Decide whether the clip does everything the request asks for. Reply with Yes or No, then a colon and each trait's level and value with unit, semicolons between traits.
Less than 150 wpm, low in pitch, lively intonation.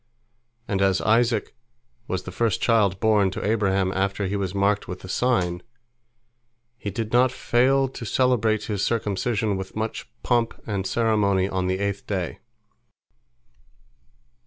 No: average, 140 wpm; low, 100 Hz; average, 3.1 semitones